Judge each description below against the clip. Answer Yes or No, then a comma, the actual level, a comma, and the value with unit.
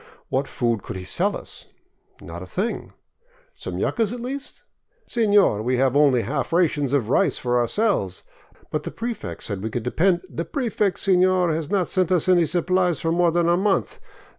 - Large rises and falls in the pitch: Yes, wide, 7.1 semitones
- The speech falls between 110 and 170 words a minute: No, average, 185 wpm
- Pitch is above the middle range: No, medium, 170 Hz